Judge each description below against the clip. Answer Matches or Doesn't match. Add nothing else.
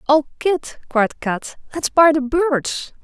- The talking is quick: Doesn't match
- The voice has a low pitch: Doesn't match